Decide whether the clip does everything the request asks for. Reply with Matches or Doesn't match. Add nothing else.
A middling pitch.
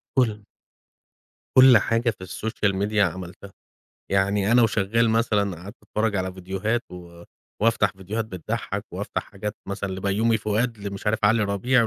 Doesn't match